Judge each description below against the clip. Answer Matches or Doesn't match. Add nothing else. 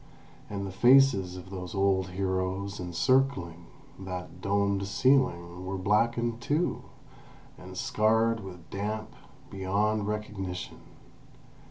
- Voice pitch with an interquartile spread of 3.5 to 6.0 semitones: Doesn't match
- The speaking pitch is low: Matches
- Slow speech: Matches